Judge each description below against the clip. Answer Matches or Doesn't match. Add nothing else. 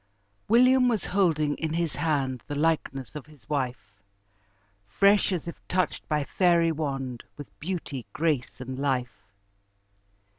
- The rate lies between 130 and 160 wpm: Matches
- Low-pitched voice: Doesn't match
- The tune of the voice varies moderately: Matches